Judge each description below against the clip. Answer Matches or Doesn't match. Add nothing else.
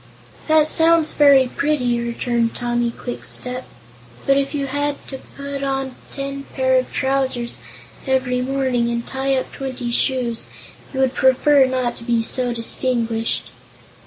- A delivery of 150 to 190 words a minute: Doesn't match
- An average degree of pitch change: Doesn't match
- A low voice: Doesn't match